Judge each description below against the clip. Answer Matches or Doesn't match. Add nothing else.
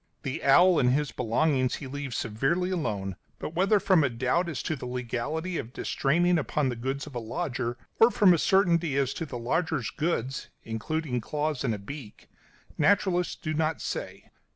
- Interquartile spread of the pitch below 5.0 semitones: Doesn't match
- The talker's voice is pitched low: Doesn't match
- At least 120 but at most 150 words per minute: Doesn't match